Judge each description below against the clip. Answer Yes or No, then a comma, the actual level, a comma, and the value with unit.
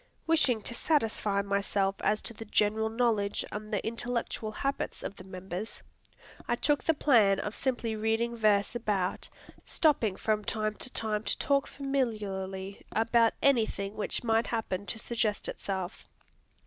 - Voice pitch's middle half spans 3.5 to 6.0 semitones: No, average, 2.8 semitones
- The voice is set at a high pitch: Yes, high, 220 Hz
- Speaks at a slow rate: No, average, 150 wpm